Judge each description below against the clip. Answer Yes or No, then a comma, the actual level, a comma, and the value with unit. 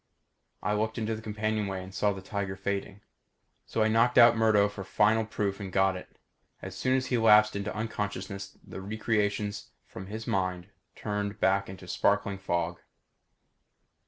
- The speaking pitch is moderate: No, low, 105 Hz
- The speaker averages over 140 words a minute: Yes, average, 160 wpm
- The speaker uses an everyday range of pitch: No, narrow, 2.1 semitones